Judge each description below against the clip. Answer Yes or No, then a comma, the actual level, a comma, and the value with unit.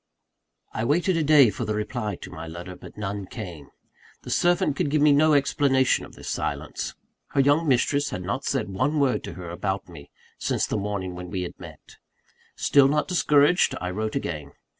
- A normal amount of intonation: No, wide, 7.8 semitones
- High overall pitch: No, low, 115 Hz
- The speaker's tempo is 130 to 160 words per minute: No, average, 195 wpm